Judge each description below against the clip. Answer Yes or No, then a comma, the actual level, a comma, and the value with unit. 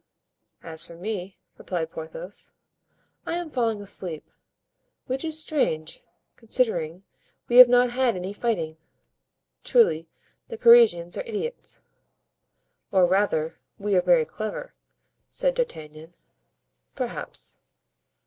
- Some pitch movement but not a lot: No, wide, 7.0 semitones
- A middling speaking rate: No, slow, 110 wpm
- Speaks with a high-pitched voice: Yes, high, 205 Hz